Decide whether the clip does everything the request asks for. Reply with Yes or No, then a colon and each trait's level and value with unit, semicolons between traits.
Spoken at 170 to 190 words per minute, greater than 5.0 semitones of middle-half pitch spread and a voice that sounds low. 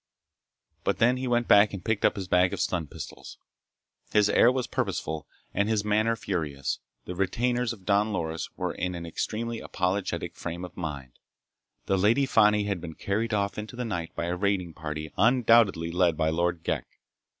No: average, 185 wpm; average, 4.5 semitones; low, 100 Hz